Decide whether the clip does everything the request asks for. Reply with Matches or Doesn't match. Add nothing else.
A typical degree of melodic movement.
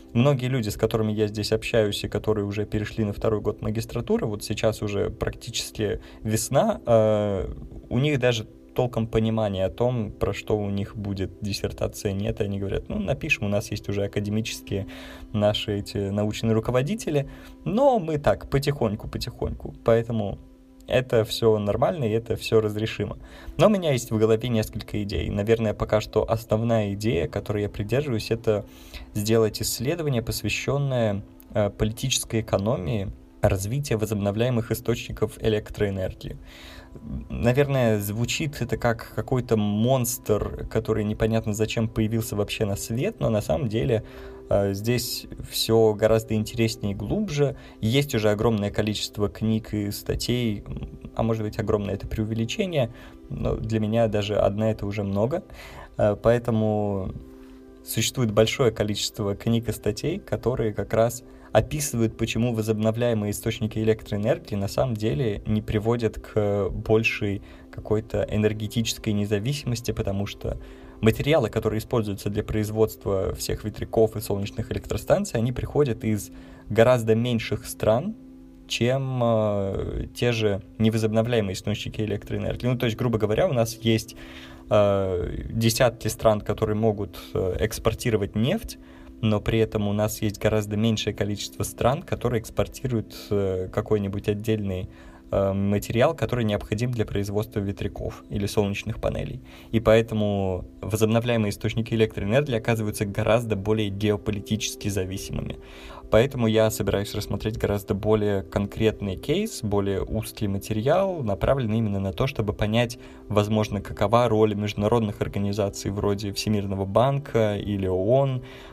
Doesn't match